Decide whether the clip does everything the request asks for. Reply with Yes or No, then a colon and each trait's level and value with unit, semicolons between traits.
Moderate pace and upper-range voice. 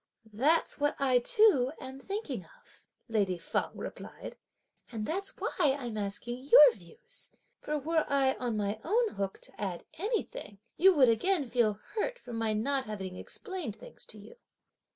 Yes: average, 160 wpm; very high, 260 Hz